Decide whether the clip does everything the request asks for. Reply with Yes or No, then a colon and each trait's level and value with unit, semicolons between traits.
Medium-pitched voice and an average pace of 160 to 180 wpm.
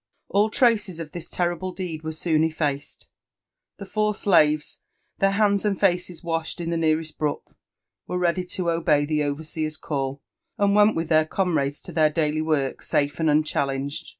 Yes: medium, 160 Hz; average, 170 wpm